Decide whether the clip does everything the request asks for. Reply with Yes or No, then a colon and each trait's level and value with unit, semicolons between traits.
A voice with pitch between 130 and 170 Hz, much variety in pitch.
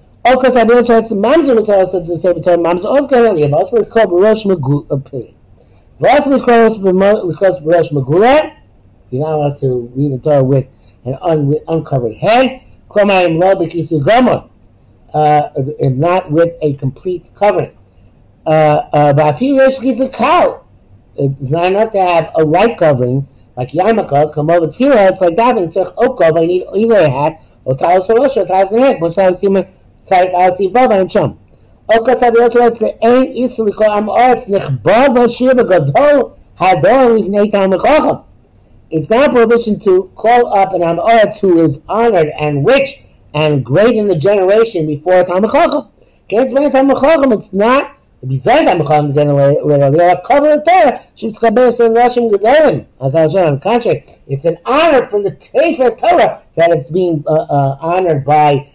No: medium, 185 Hz; wide, 7.7 semitones